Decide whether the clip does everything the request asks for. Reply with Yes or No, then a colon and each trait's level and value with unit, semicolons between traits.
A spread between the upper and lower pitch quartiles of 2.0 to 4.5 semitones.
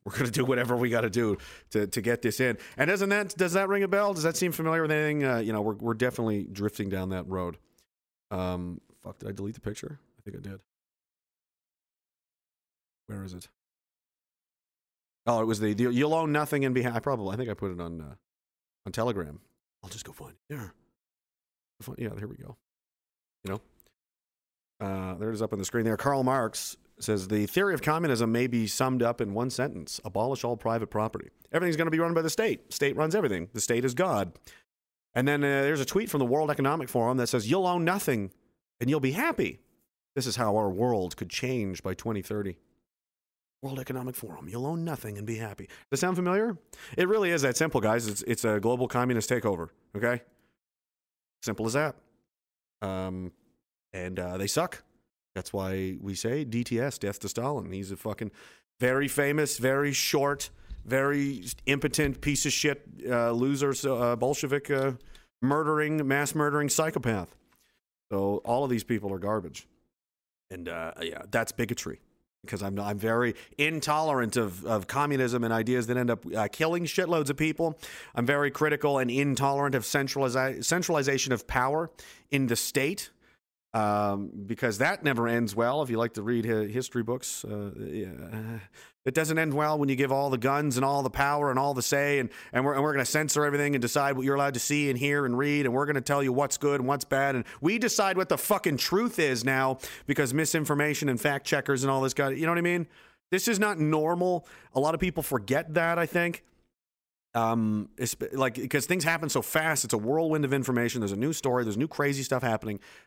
No: average, 5.1 semitones